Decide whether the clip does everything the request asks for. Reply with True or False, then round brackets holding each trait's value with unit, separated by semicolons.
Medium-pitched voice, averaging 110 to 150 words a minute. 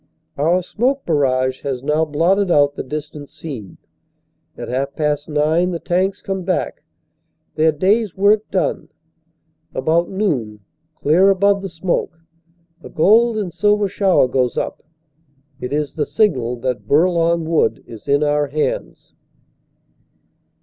True (160 Hz; 135 wpm)